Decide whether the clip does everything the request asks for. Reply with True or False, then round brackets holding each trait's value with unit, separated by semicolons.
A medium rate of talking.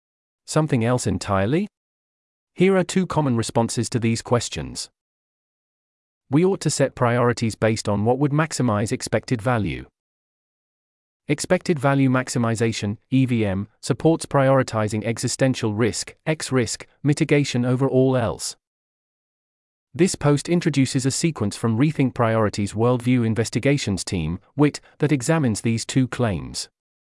False (120 wpm)